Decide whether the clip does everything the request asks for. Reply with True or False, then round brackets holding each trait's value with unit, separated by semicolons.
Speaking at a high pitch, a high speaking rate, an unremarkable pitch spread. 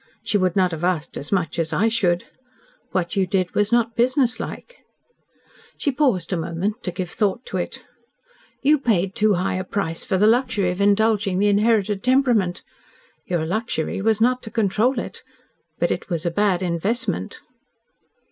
False (200 Hz; 170 wpm; 4.0 semitones)